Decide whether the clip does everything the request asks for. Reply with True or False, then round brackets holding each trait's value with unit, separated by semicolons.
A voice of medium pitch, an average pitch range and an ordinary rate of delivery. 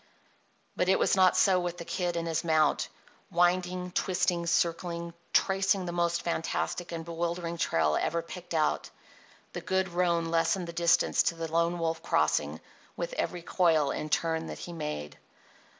False (170 Hz; 1.4 semitones; 165 wpm)